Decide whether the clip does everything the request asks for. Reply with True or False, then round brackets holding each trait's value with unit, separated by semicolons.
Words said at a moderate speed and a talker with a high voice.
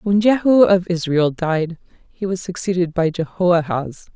False (145 wpm; 175 Hz)